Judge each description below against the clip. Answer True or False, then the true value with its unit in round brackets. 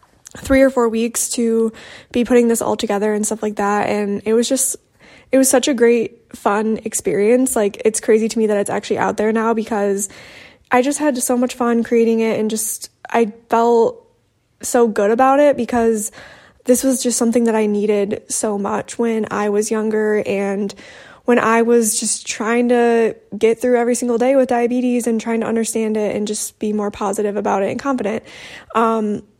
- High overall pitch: True (230 Hz)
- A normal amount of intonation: False (2.2 semitones)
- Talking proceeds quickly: False (195 wpm)